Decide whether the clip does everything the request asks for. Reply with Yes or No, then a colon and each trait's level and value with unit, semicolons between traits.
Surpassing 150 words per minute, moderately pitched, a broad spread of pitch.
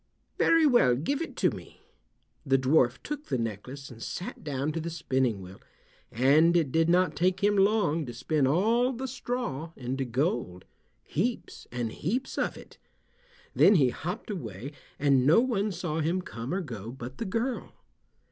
Yes: average, 165 wpm; medium, 155 Hz; wide, 7.4 semitones